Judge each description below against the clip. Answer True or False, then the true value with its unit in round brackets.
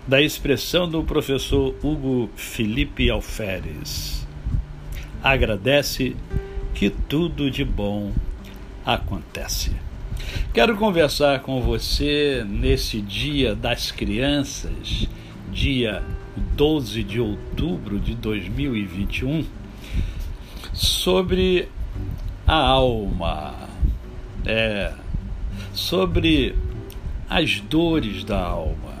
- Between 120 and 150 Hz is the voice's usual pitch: False (110 Hz)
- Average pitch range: False (5.7 semitones)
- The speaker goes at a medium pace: False (75 wpm)